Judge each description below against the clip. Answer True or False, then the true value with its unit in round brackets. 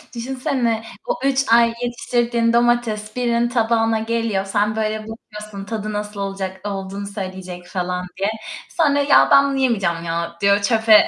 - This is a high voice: True (215 Hz)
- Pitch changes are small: False (3.1 semitones)